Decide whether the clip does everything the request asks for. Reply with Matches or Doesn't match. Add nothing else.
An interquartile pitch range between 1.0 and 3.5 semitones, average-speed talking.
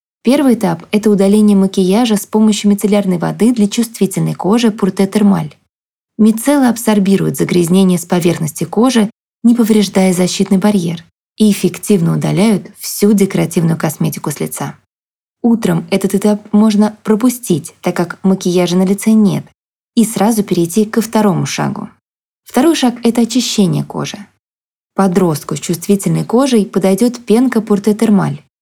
Matches